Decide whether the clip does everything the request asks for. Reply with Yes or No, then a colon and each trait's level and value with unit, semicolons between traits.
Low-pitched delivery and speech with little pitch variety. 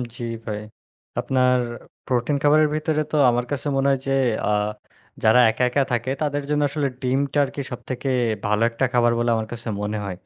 No: low, 125 Hz; average, 3.2 semitones